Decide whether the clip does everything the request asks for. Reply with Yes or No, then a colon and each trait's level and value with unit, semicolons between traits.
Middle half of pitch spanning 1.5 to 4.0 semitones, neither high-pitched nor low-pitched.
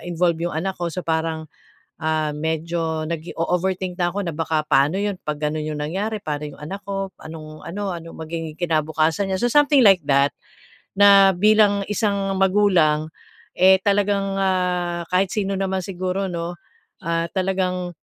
Yes: average, 3.4 semitones; medium, 180 Hz